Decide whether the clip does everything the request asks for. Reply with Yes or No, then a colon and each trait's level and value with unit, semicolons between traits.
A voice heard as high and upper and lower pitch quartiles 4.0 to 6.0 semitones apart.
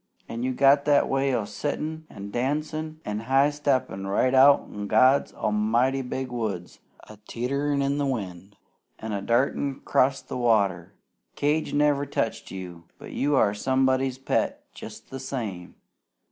No: low, 130 Hz; average, 4.8 semitones